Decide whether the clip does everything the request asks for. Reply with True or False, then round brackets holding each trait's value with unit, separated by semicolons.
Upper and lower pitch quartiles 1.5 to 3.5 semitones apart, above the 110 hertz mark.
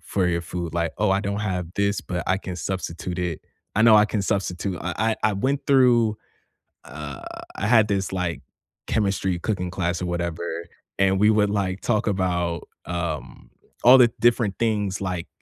False (3.2 semitones; 95 Hz)